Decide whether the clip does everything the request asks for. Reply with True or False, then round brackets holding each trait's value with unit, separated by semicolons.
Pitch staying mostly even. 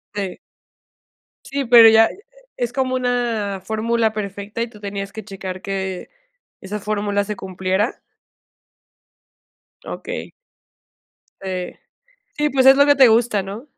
False (3.6 semitones)